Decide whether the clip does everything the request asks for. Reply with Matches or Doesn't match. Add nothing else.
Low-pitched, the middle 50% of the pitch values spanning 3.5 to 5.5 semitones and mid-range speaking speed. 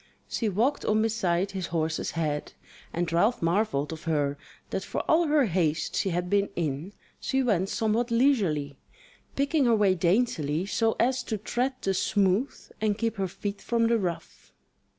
Doesn't match